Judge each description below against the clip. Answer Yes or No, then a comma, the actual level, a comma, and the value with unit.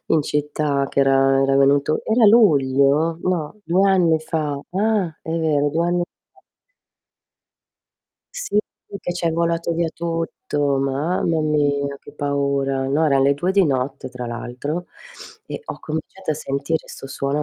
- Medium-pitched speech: Yes, medium, 150 Hz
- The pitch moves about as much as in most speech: Yes, average, 3.3 semitones